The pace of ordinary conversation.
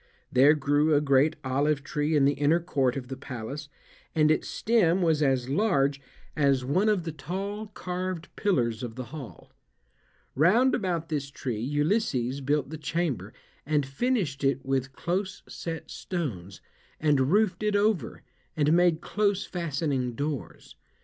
Yes: average, 150 wpm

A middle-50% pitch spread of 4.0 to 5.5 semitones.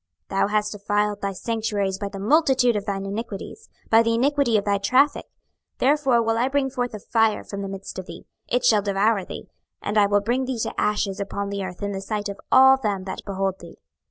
No: average, 3.4 semitones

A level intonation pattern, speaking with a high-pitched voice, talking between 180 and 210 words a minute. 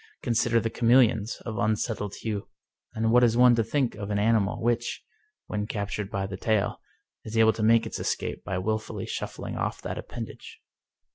No: narrow, 2.0 semitones; low, 110 Hz; average, 185 wpm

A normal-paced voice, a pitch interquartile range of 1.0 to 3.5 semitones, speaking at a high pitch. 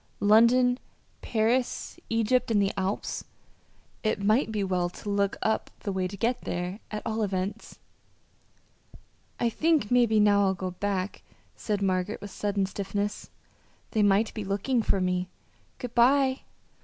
Yes: average, 145 wpm; average, 2.9 semitones; high, 205 Hz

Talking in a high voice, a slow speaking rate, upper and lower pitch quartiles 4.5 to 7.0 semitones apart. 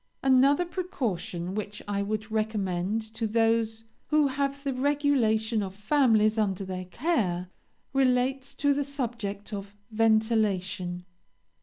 Yes: high, 220 Hz; slow, 120 wpm; average, 5.0 semitones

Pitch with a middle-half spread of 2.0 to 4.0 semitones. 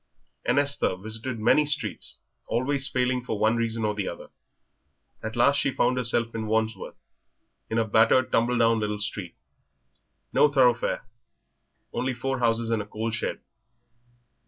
Yes: narrow, 2.5 semitones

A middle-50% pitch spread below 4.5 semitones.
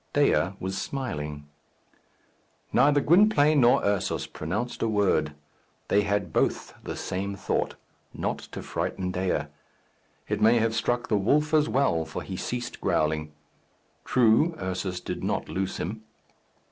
No: average, 5.3 semitones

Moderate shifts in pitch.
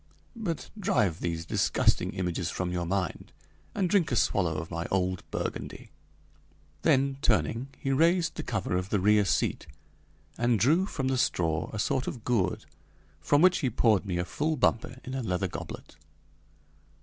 No: wide, 7.1 semitones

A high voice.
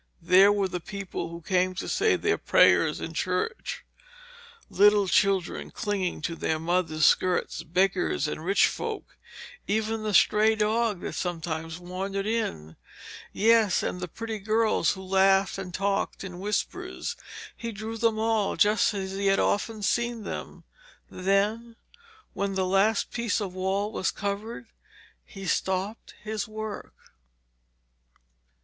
Yes: high, 200 Hz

